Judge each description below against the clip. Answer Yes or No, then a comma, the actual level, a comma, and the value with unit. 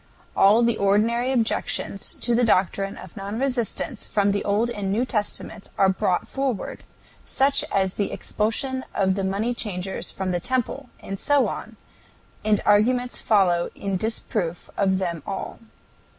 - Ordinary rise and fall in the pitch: Yes, average, 3.6 semitones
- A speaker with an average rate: Yes, average, 150 wpm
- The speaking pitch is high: Yes, high, 205 Hz